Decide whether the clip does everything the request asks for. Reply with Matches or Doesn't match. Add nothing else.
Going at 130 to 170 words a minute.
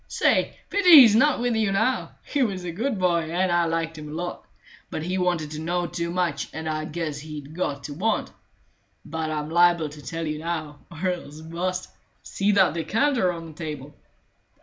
Doesn't match